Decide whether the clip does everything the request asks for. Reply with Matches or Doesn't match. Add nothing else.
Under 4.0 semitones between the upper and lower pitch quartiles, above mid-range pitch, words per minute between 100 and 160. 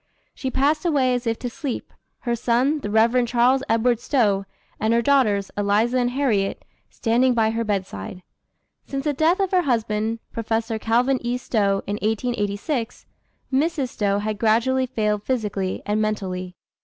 Matches